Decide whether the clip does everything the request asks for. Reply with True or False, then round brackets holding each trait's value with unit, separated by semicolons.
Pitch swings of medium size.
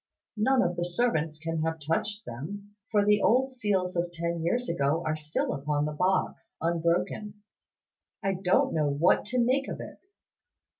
True (4.4 semitones)